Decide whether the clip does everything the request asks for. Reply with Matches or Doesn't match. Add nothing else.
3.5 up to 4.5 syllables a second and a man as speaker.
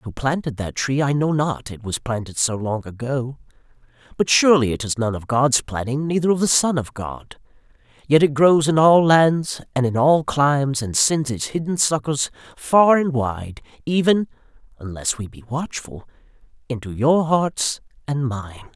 Matches